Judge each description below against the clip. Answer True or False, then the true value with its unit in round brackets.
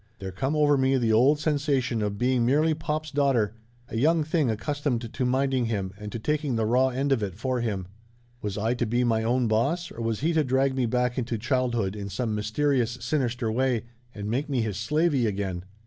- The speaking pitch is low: True (125 Hz)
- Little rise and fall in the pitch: False (4.1 semitones)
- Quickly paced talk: True (215 wpm)